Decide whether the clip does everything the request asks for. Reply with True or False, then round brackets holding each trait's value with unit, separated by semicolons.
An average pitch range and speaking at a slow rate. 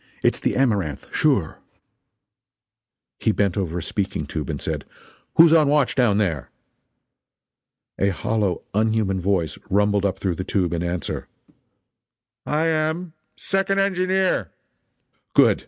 False (9.0 semitones; 125 wpm)